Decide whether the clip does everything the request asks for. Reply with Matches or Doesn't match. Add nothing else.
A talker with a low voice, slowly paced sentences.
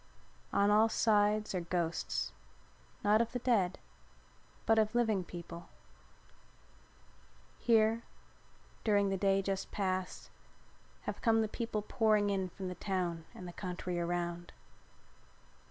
Doesn't match